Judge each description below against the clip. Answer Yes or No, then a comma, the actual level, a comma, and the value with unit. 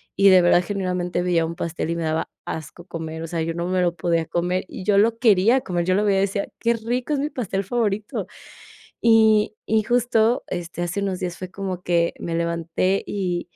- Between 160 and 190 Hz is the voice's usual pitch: Yes, medium, 185 Hz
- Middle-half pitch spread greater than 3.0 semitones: Yes, average, 3.6 semitones